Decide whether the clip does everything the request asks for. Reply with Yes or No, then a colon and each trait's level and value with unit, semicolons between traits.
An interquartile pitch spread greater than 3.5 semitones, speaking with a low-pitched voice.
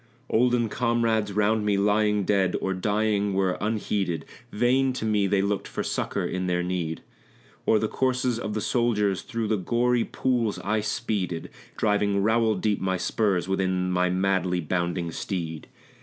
No: average, 3.1 semitones; low, 105 Hz